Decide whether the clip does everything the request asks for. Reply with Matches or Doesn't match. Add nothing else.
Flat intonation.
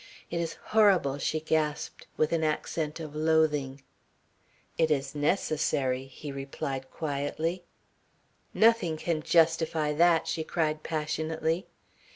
Matches